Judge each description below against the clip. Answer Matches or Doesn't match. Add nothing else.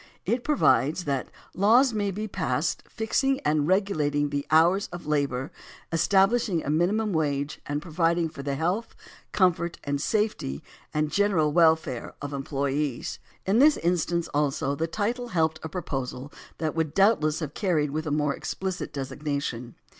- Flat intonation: Doesn't match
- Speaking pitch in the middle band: Matches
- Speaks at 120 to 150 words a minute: Matches